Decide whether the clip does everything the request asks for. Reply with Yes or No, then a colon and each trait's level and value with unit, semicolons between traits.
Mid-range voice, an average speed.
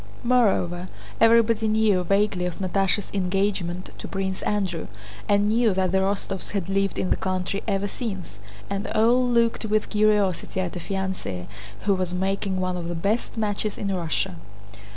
No: high, 195 Hz; average, 160 wpm